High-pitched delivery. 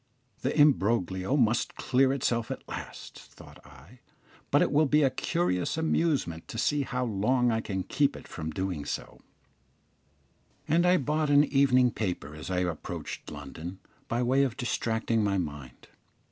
No: low, 120 Hz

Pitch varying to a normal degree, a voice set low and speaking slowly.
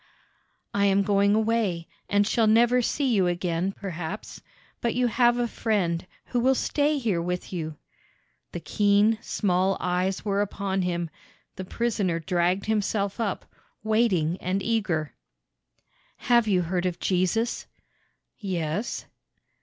No: average, 3.8 semitones; high, 200 Hz; slow, 130 wpm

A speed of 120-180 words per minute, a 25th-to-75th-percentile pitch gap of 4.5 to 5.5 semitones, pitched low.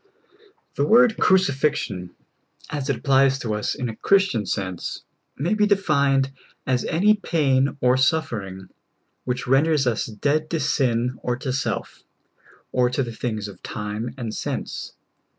Yes: average, 150 wpm; average, 4.8 semitones; low, 130 Hz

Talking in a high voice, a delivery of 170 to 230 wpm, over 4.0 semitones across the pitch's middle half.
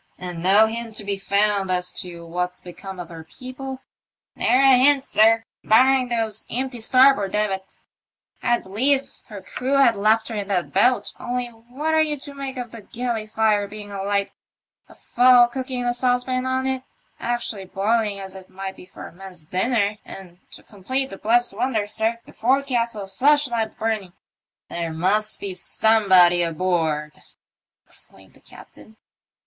Yes: high, 220 Hz; average, 180 wpm; average, 4.5 semitones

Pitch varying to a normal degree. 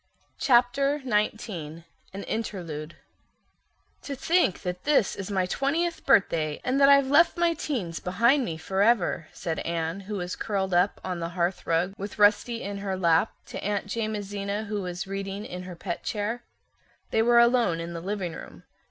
Yes: average, 5.0 semitones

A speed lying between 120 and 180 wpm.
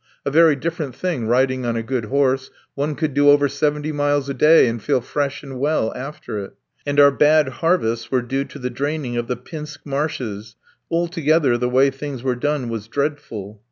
No: average, 195 wpm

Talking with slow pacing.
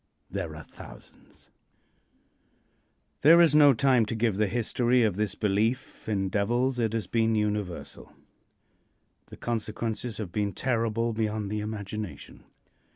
Yes: slow, 130 wpm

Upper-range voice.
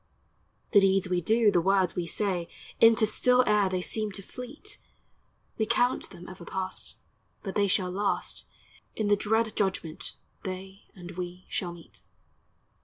Yes: high, 195 Hz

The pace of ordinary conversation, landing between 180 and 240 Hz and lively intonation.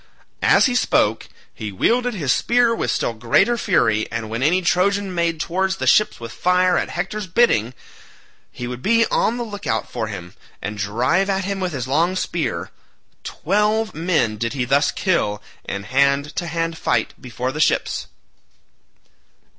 No: average, 170 wpm; medium, 165 Hz; wide, 8.3 semitones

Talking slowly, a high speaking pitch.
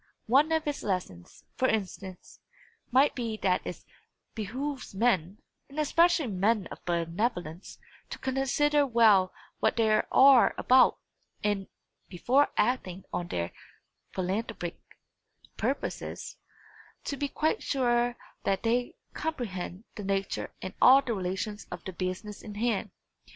Yes: slow, 125 wpm; high, 220 Hz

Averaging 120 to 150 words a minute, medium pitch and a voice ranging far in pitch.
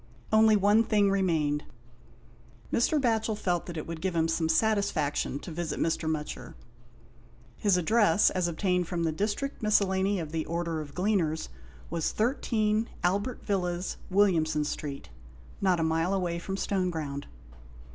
No: average, 145 wpm; medium, 180 Hz; average, 4.2 semitones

